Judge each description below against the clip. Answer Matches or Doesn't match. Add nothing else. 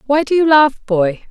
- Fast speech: Matches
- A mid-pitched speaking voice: Doesn't match